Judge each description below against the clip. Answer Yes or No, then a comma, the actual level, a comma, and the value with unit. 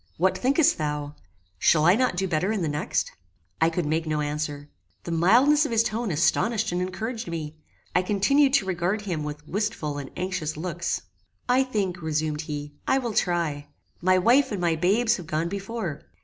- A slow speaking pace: No, average, 185 wpm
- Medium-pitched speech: Yes, medium, 180 Hz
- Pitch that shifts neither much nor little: No, wide, 5.9 semitones